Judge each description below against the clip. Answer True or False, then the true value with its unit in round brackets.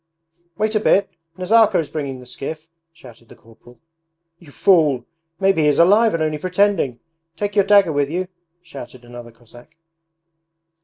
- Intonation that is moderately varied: False (7.3 semitones)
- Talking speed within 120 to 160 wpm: True (155 wpm)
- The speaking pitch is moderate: True (155 Hz)